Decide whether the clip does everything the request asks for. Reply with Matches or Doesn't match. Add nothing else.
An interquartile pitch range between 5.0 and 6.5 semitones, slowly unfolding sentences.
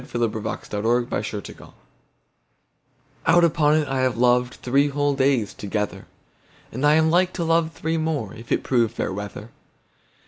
Matches